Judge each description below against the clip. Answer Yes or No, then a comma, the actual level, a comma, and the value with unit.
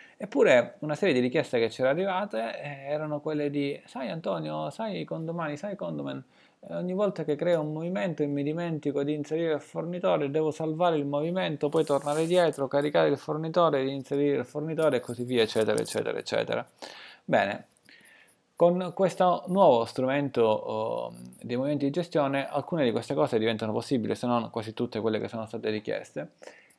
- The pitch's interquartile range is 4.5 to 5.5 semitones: Yes, average, 5.1 semitones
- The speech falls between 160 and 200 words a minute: Yes, fast, 170 wpm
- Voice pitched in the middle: Yes, medium, 145 Hz